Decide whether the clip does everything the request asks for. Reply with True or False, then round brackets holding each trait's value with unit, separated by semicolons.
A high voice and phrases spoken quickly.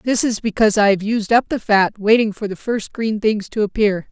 True (215 Hz; 250 wpm)